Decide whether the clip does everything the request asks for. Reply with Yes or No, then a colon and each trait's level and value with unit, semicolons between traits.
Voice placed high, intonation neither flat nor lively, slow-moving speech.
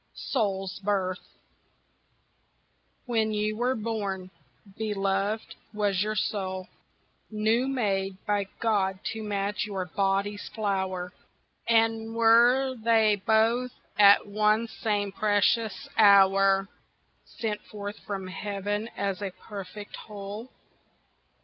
No: high, 205 Hz; narrow, 2.1 semitones; slow, 100 wpm